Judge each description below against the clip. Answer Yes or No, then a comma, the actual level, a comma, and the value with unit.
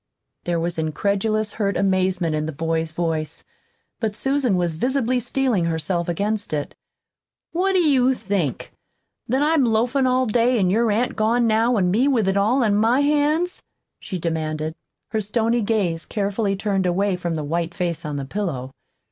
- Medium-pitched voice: No, high, 205 Hz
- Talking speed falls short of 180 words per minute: Yes, average, 170 wpm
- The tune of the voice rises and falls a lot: Yes, wide, 5.9 semitones